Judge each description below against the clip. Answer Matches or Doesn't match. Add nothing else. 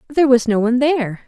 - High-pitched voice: Matches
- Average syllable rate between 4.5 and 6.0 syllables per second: Doesn't match